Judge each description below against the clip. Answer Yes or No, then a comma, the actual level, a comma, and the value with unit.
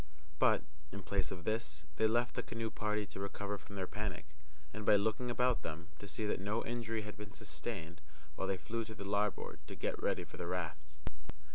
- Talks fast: Yes, fast, 210 wpm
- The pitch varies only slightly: No, average, 3.1 semitones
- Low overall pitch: Yes, low, 105 Hz